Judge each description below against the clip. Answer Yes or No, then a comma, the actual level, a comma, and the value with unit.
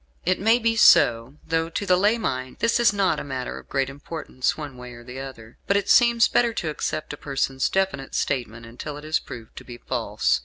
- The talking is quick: Yes, fast, 225 wpm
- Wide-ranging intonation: Yes, wide, 7.3 semitones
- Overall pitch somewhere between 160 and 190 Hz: No, medium, 145 Hz